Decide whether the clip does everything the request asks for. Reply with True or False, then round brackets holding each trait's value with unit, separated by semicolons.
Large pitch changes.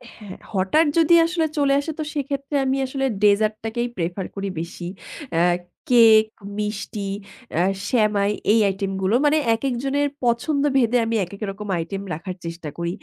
True (5.8 semitones)